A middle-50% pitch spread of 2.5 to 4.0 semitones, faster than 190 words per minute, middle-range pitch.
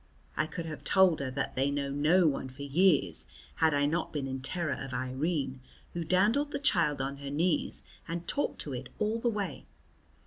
No: average, 4.8 semitones; average, 200 wpm; medium, 150 Hz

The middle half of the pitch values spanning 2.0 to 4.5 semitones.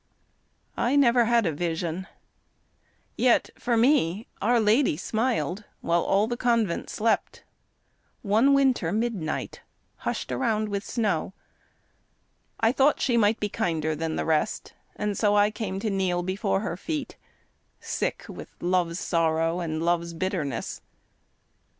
No: wide, 5.4 semitones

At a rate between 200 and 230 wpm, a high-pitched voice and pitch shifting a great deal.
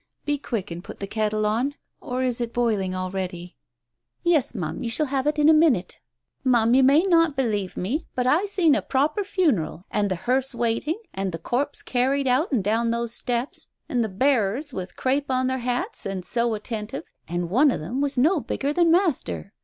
Yes: fast, 205 wpm; high, 245 Hz; wide, 5.8 semitones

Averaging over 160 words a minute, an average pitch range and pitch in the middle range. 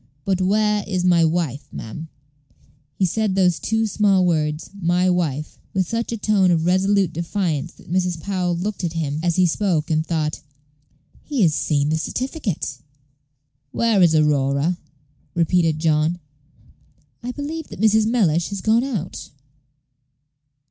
No: average, 145 wpm; average, 4.3 semitones; medium, 180 Hz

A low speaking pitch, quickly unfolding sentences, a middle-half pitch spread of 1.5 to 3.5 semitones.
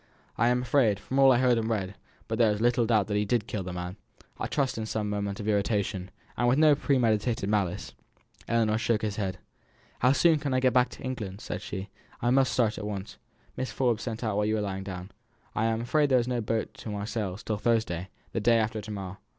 Yes: low, 110 Hz; fast, 230 wpm; average, 3.1 semitones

